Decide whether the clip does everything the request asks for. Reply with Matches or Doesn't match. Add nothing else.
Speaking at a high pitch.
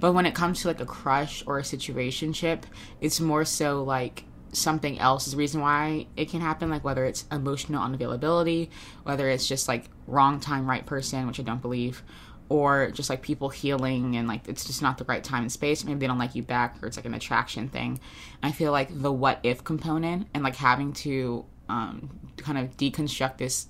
Doesn't match